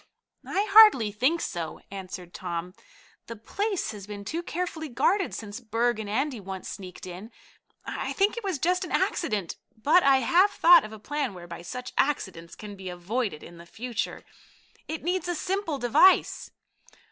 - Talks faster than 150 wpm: Yes, average, 170 wpm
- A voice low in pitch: No, high, 235 Hz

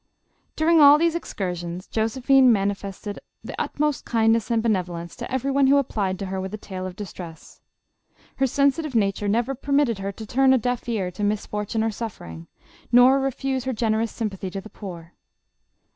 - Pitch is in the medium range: No, high, 220 Hz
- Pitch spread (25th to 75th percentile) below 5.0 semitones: No, average, 5.3 semitones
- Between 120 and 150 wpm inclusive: No, average, 180 wpm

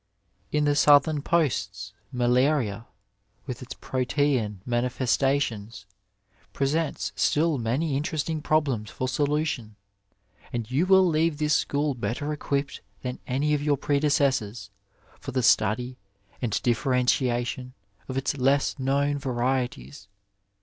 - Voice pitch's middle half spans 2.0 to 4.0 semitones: Yes, average, 3.3 semitones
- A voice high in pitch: No, low, 135 Hz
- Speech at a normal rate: No, slow, 120 wpm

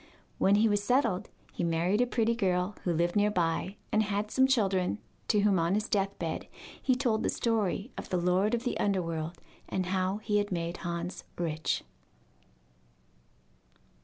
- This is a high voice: Yes, high, 195 Hz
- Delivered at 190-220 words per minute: No, average, 170 wpm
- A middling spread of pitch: Yes, average, 3.4 semitones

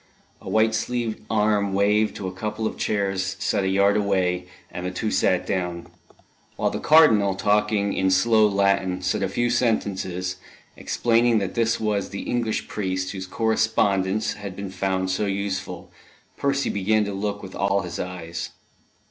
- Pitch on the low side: Yes, low, 100 Hz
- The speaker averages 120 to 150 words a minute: No, average, 165 wpm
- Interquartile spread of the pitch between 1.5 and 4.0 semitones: Yes, narrow, 2.5 semitones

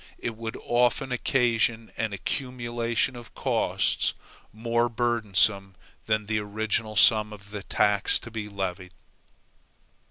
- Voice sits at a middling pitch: No, low, 110 Hz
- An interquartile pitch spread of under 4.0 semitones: Yes, narrow, 2.4 semitones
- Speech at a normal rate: No, slow, 120 wpm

